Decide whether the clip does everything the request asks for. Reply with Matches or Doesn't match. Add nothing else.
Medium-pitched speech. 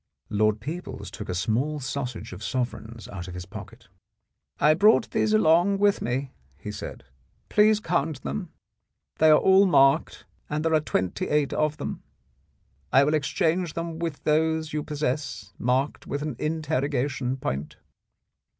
Matches